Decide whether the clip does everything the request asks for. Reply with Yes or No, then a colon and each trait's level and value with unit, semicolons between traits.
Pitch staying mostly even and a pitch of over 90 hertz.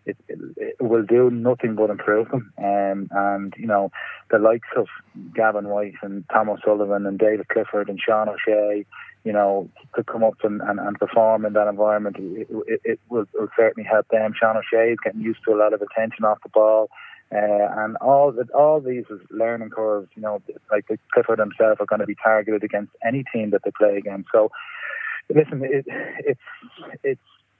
Yes: narrow, 1.9 semitones; low, 110 Hz